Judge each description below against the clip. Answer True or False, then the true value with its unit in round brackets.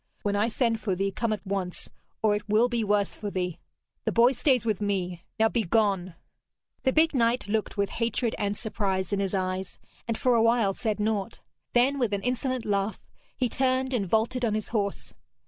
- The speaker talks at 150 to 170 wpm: False (200 wpm)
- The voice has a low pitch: False (215 Hz)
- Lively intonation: False (3.2 semitones)